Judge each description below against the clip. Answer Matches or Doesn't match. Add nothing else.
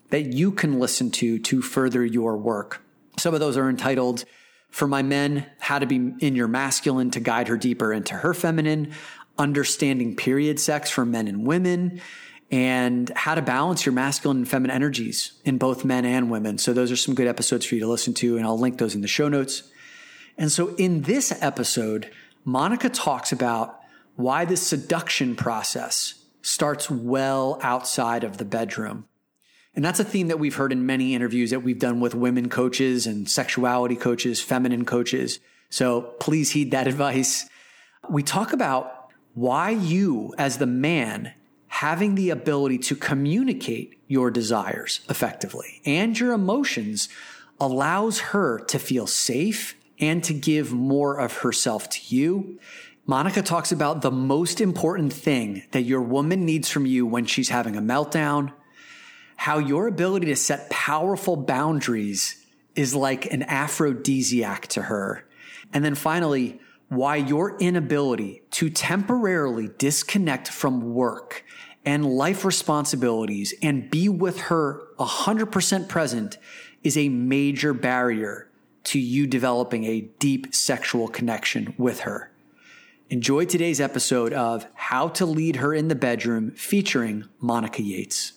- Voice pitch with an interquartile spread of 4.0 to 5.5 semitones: Matches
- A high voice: Doesn't match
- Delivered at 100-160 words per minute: Matches